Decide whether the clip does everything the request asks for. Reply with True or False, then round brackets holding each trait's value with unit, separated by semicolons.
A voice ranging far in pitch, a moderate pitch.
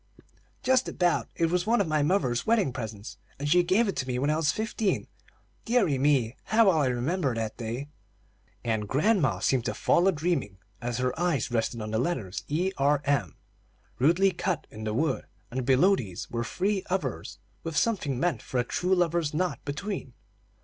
True (6.9 semitones; 145 Hz)